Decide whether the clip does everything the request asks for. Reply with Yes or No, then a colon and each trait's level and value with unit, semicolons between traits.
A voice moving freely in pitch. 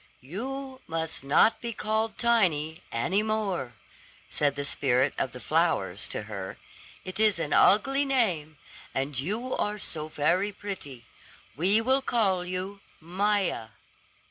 Yes: wide, 6.7 semitones